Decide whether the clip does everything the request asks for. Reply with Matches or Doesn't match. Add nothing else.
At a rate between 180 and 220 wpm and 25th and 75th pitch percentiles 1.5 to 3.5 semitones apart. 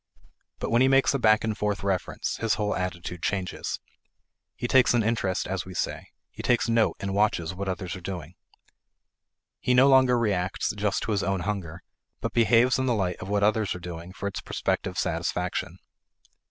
Doesn't match